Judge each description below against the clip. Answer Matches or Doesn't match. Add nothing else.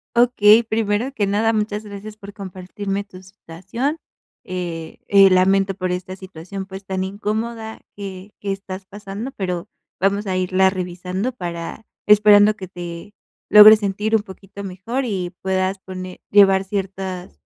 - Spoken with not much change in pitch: Matches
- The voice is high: Matches